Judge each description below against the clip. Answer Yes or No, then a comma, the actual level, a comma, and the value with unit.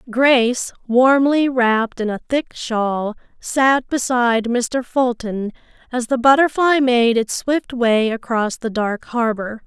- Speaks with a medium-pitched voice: No, high, 240 Hz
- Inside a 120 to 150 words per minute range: Yes, slow, 135 wpm